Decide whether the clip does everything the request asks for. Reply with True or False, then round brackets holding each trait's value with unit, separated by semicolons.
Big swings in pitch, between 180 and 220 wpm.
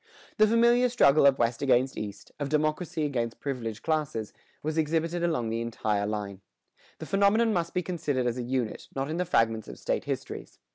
True (6.5 semitones; 185 wpm)